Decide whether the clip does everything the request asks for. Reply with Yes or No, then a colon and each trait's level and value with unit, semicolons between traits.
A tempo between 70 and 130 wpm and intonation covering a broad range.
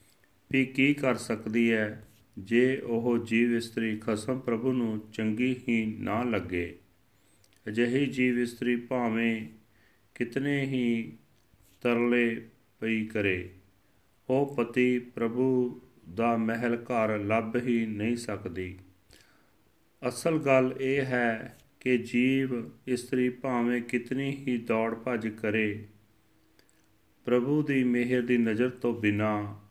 No: average, 110 wpm; narrow, 2.6 semitones